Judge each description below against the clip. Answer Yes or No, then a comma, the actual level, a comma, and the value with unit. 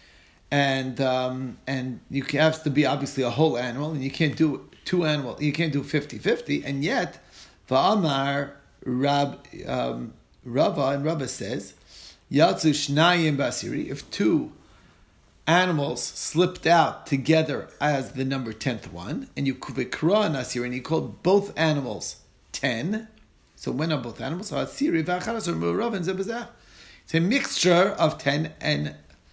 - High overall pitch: No, medium, 140 Hz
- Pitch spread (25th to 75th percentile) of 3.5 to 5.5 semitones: Yes, average, 4.2 semitones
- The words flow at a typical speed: No, slow, 125 wpm